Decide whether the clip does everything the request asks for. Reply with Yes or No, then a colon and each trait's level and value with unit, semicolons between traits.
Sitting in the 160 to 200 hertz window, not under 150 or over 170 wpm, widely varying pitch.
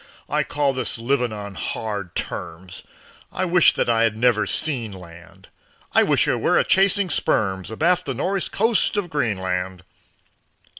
No: low, 115 Hz; average, 155 wpm; wide, 8.8 semitones